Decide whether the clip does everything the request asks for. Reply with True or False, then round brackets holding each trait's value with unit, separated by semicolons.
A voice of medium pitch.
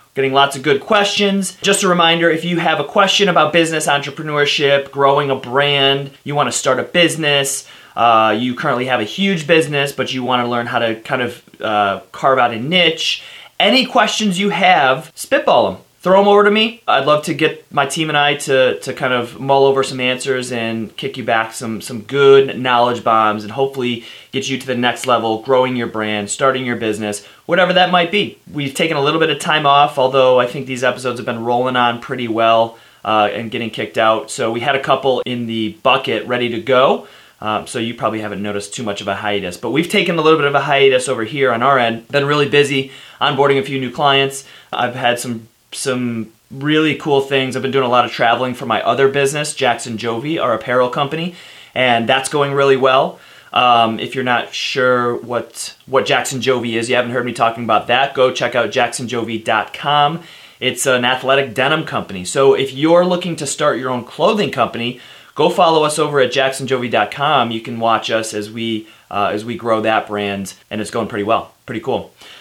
False (130 Hz)